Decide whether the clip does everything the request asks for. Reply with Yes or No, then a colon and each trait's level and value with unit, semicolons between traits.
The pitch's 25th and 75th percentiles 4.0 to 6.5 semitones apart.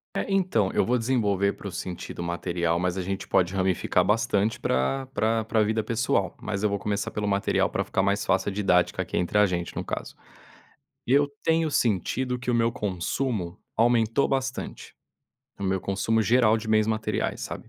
No: average, 3.5 semitones